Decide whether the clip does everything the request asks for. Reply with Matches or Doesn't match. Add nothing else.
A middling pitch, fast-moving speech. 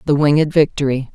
Doesn't match